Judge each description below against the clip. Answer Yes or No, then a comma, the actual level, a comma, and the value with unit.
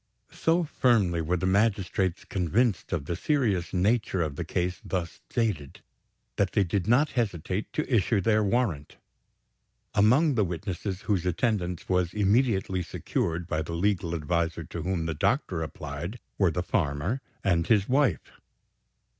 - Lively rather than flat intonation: No, average, 4.4 semitones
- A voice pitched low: Yes, very low, 95 Hz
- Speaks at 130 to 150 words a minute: Yes, average, 145 wpm